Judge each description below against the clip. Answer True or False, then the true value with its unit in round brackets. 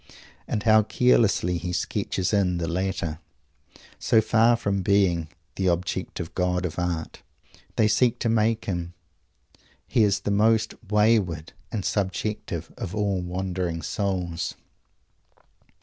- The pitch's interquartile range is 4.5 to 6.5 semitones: False (3.4 semitones)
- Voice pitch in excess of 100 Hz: False (95 Hz)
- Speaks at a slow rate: True (125 wpm)